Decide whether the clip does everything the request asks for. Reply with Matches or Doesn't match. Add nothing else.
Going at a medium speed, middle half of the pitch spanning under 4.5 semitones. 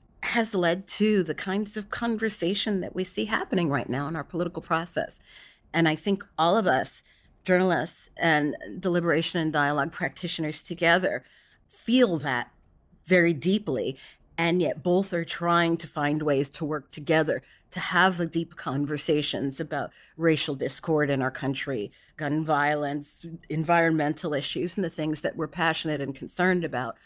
Matches